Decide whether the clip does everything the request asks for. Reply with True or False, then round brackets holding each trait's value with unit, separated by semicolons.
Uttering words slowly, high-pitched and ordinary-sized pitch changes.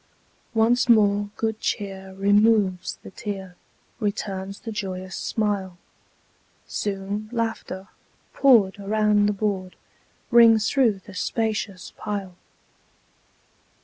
False (95 wpm; 205 Hz; 2.3 semitones)